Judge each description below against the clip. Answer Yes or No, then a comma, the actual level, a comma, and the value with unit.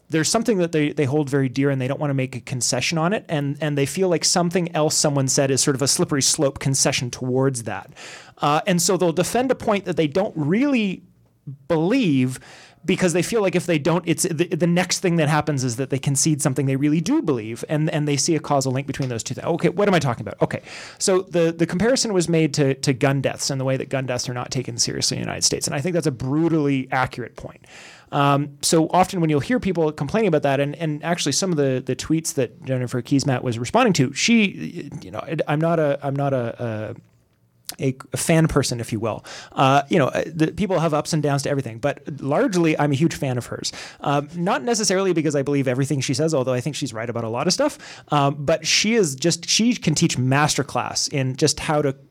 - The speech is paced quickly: Yes, fast, 245 wpm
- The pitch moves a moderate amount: Yes, average, 4.0 semitones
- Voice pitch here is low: No, medium, 150 Hz